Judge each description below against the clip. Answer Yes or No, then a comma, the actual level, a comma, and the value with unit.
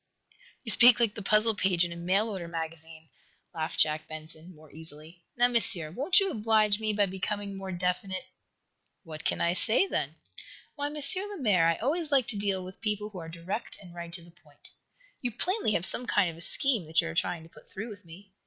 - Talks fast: Yes, fast, 215 wpm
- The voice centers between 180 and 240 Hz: Yes, high, 190 Hz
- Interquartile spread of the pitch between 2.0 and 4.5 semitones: No, average, 4.9 semitones